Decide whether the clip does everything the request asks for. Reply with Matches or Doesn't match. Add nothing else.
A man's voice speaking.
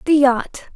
Doesn't match